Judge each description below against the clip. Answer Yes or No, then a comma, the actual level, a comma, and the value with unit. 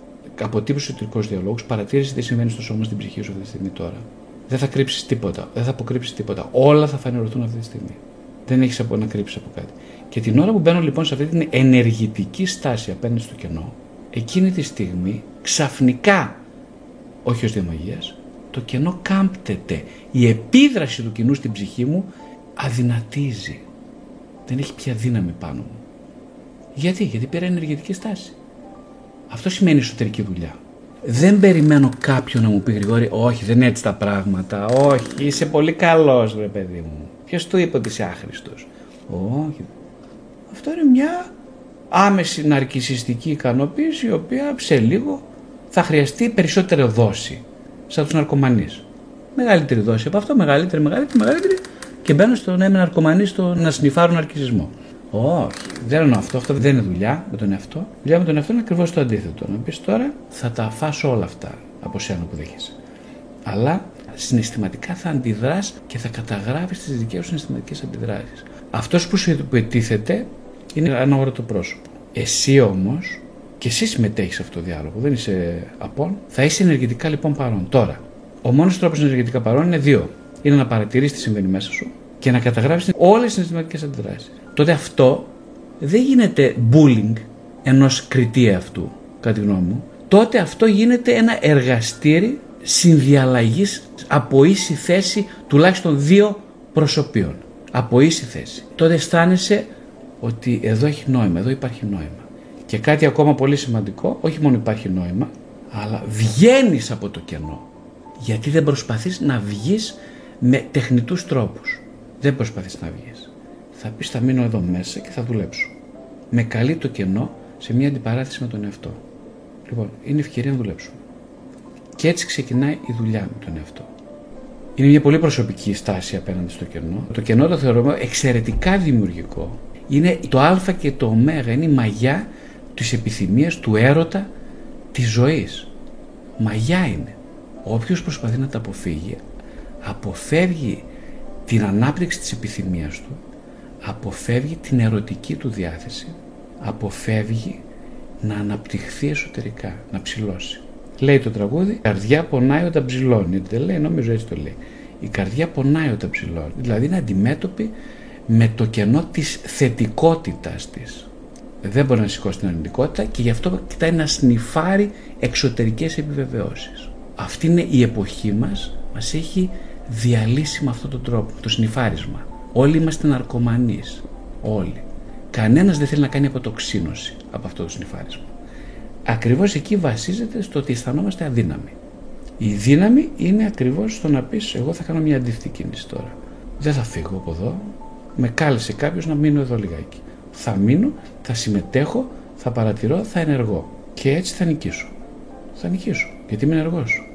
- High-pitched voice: No, low, 135 Hz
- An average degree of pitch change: No, wide, 7.1 semitones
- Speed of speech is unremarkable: Yes, average, 155 wpm